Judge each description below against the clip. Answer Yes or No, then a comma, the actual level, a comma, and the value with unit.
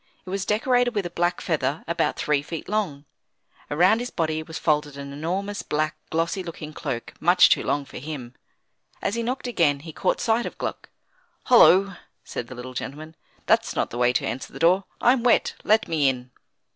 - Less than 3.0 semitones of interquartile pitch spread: No, wide, 5.5 semitones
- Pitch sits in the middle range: Yes, medium, 165 Hz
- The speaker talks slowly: No, average, 195 wpm